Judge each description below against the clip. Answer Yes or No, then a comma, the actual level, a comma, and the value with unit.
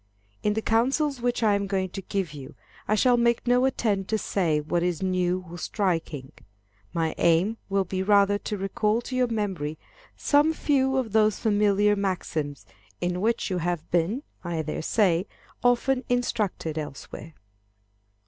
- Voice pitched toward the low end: No, high, 200 Hz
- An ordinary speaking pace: Yes, average, 160 wpm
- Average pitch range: Yes, average, 4.8 semitones